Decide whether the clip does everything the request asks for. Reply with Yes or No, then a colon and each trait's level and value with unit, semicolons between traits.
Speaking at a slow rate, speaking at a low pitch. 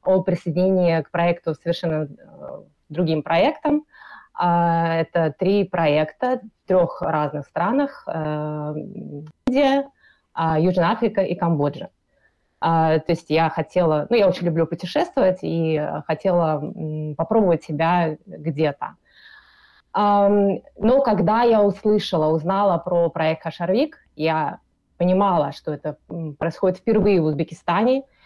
No: slow, 105 wpm; medium, 170 Hz